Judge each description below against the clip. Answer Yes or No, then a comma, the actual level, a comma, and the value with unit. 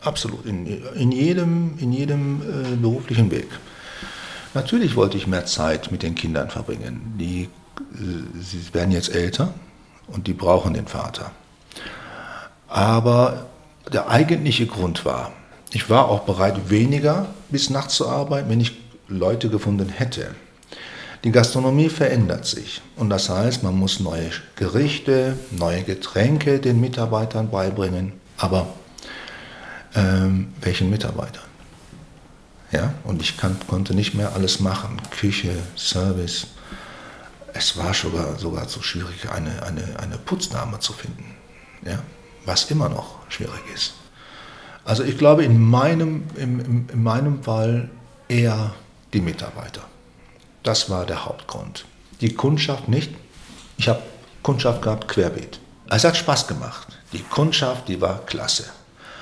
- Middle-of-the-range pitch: No, low, 110 Hz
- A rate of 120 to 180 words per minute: Yes, average, 130 wpm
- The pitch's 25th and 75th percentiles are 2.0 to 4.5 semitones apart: No, wide, 5.4 semitones